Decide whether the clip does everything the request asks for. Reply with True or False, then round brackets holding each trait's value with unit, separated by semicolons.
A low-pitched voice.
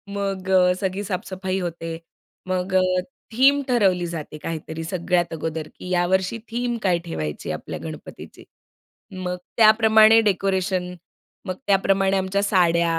False (185 Hz)